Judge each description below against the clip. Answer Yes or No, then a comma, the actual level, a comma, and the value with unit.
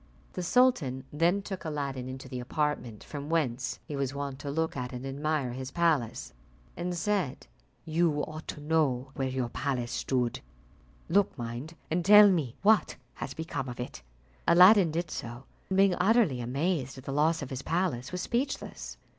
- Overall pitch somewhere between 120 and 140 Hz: No, medium, 150 Hz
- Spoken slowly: No, average, 170 wpm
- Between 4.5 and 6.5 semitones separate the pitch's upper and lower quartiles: Yes, average, 4.9 semitones